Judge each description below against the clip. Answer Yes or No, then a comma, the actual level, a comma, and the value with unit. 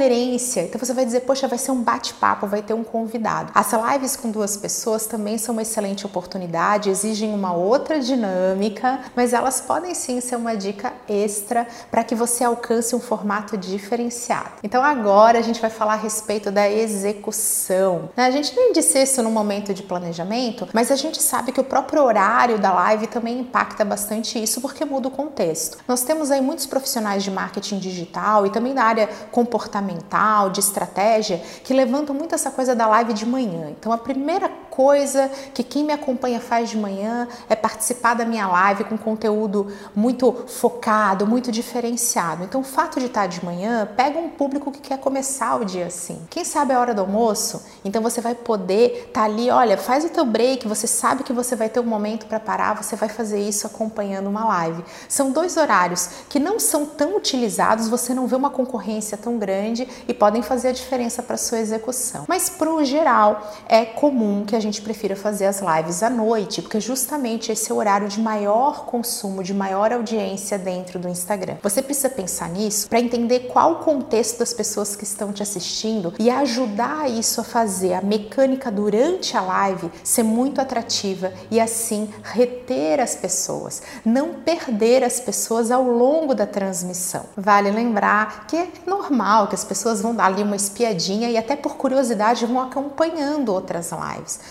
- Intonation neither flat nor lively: Yes, average, 3.7 semitones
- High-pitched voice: Yes, high, 230 Hz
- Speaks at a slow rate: No, fast, 185 wpm